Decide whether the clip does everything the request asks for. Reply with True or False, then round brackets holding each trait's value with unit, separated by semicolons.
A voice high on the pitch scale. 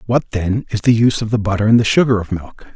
False (110 Hz)